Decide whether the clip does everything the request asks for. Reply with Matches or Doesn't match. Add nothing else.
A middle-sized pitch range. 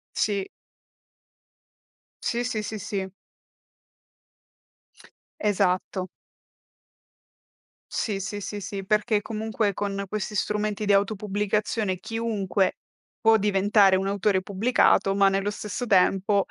Doesn't match